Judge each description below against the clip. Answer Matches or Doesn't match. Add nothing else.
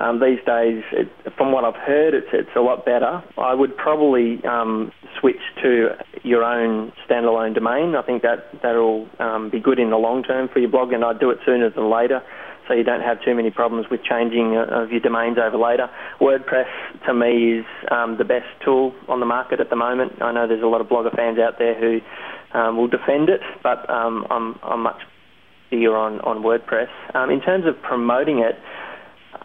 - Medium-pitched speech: Doesn't match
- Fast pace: Matches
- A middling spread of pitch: Doesn't match